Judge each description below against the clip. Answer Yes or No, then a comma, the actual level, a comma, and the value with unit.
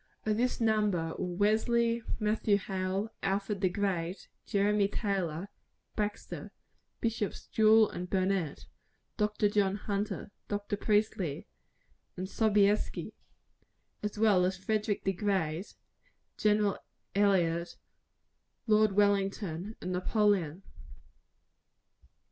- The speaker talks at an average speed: No, slow, 95 wpm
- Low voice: No, high, 200 Hz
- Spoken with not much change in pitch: Yes, narrow, 2.1 semitones